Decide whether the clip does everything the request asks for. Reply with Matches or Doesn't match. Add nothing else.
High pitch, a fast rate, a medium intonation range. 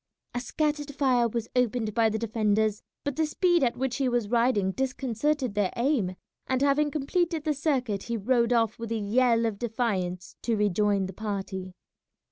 Doesn't match